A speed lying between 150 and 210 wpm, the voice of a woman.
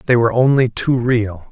No: average, 200 wpm; male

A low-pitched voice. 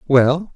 No: medium, 150 Hz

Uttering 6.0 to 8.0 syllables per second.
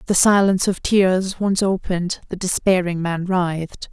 No: 4.7 syllables/s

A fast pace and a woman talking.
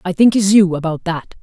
Yes: fast, 255 wpm; female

